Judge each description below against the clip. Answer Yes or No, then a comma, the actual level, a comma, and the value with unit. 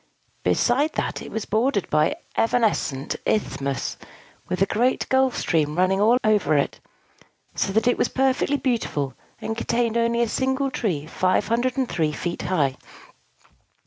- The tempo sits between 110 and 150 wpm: Yes, average, 145 wpm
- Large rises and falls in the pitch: Yes, wide, 6.7 semitones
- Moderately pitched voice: No, high, 220 Hz